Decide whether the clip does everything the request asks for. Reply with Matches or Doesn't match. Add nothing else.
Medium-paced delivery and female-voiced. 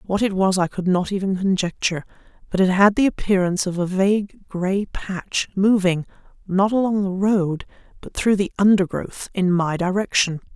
Matches